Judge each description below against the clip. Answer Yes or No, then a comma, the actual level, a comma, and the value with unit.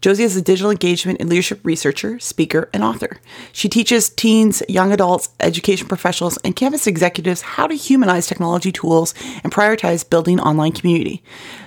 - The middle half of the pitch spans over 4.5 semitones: No, average, 3.9 semitones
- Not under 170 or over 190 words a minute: No, average, 160 wpm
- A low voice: No, medium, 185 Hz